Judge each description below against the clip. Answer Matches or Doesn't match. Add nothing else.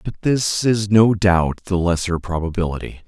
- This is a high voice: Doesn't match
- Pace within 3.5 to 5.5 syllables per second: Matches